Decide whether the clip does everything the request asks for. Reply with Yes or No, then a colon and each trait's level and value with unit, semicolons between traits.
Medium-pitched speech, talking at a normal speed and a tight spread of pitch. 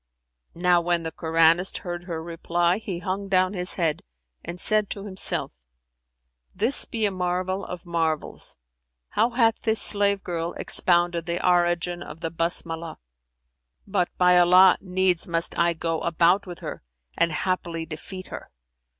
Yes: medium, 175 Hz; average, 155 wpm; narrow, 2.0 semitones